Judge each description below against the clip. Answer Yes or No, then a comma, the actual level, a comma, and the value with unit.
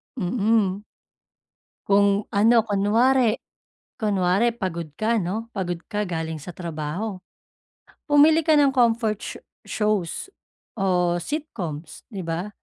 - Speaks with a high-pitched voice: Yes, high, 205 Hz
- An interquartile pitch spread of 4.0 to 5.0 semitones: Yes, average, 4.4 semitones